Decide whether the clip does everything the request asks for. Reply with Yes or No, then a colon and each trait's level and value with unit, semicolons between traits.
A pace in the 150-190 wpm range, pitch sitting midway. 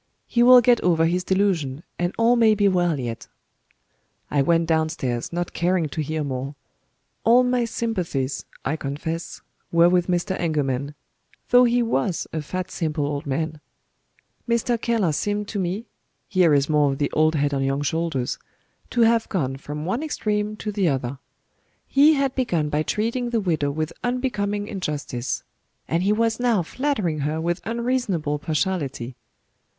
Yes: average, 160 wpm; medium, 175 Hz